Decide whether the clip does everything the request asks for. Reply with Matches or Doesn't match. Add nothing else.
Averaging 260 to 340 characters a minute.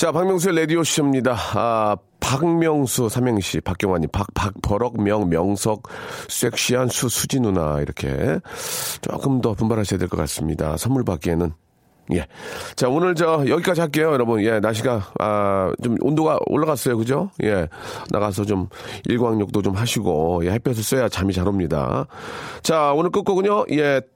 Matches